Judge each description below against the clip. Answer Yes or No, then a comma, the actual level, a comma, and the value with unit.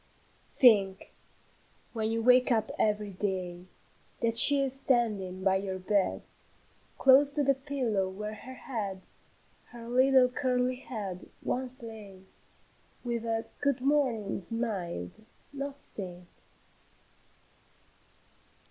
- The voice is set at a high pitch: Yes, high, 230 Hz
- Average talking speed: No, slow, 110 wpm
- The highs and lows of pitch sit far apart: No, average, 4.8 semitones